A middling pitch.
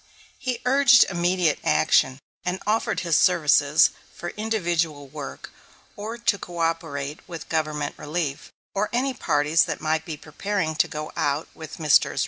Yes: medium, 165 Hz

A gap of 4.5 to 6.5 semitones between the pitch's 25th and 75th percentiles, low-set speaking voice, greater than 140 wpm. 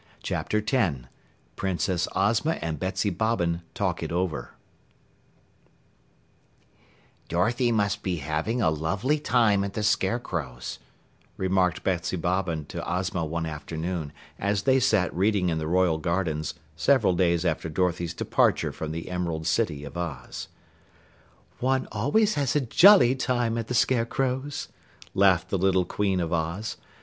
No: average, 5.2 semitones; very low, 95 Hz; slow, 135 wpm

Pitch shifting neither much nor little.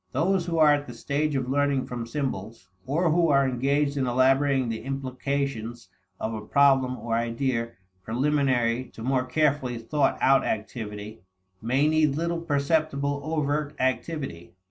Yes: average, 3.5 semitones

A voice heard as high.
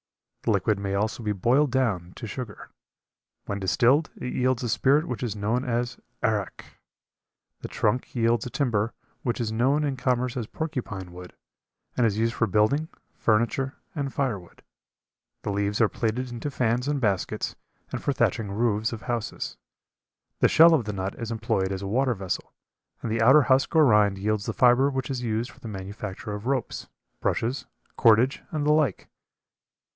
No: low, 115 Hz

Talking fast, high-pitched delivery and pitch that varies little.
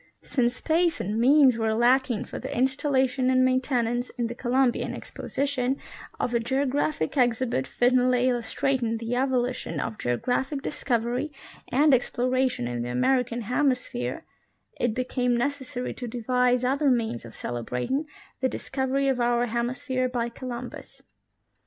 No: average, 140 wpm; very high, 250 Hz; narrow, 1.8 semitones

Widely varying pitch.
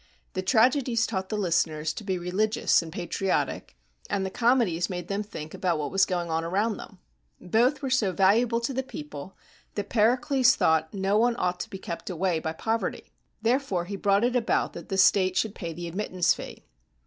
No: average, 4.5 semitones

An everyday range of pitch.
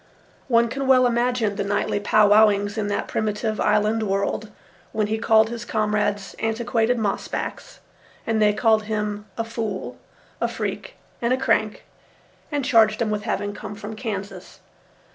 No: narrow, 1.8 semitones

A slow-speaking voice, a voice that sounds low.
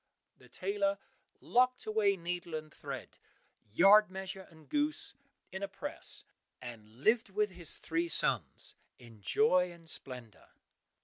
No: slow, 130 wpm; medium, 180 Hz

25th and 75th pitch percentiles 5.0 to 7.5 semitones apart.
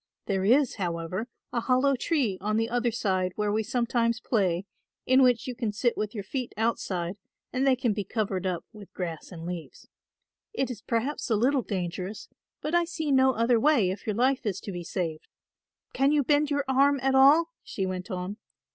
Yes: wide, 5.6 semitones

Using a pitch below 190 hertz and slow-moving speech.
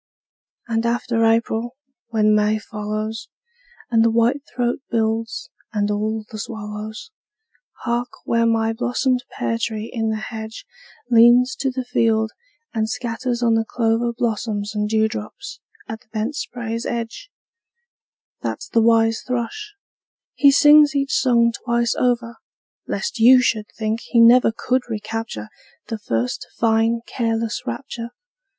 No: high, 230 Hz; slow, 130 wpm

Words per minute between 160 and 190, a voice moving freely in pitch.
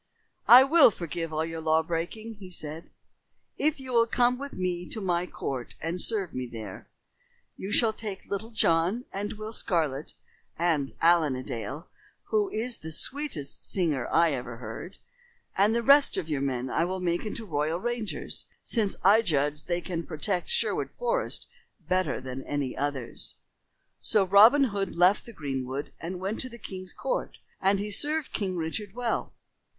Yes: average, 170 wpm; wide, 6.0 semitones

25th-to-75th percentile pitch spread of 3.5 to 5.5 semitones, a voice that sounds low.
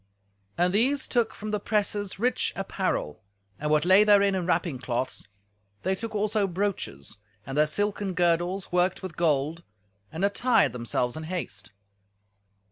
No: average, 5.0 semitones; medium, 185 Hz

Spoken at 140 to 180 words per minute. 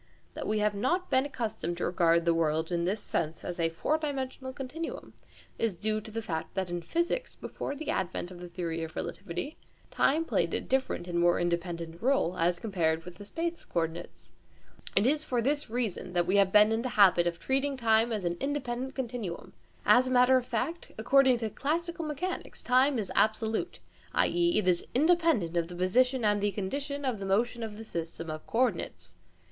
No: average, 195 wpm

